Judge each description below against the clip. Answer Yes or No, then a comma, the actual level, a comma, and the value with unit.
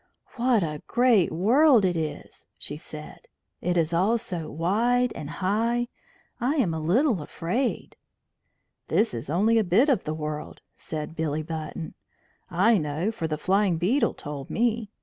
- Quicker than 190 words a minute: No, average, 155 wpm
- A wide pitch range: Yes, wide, 6.6 semitones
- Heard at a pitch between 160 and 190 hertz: Yes, medium, 185 Hz